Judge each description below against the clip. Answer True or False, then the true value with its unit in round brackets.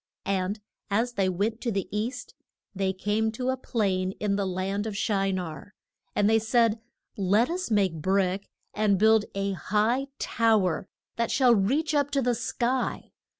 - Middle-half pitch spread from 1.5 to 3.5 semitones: True (3.2 semitones)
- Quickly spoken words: False (170 wpm)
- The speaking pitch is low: False (210 Hz)